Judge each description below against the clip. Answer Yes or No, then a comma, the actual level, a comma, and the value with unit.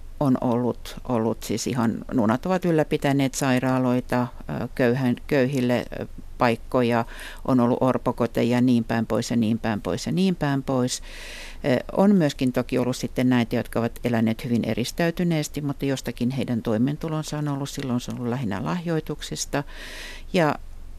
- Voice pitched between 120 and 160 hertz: Yes, low, 125 Hz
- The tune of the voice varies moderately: Yes, average, 3.1 semitones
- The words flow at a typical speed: Yes, average, 145 wpm